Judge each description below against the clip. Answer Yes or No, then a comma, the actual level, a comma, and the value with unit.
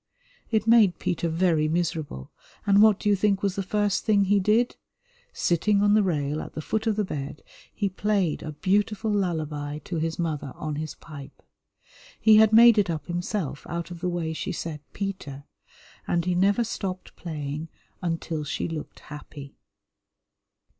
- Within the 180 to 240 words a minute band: No, average, 170 wpm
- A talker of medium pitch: Yes, medium, 175 Hz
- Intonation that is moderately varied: Yes, average, 4.8 semitones